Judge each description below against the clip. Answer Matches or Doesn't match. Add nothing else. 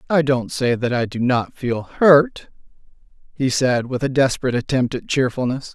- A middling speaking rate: Matches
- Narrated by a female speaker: Doesn't match